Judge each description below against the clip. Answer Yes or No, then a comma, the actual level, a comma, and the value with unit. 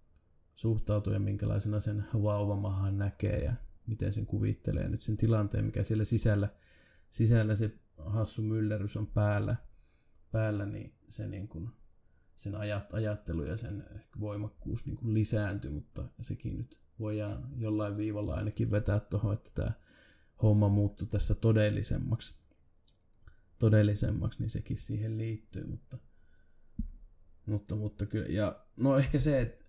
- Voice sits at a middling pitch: No, low, 105 Hz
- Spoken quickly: No, average, 130 wpm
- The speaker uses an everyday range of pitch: No, narrow, 1.5 semitones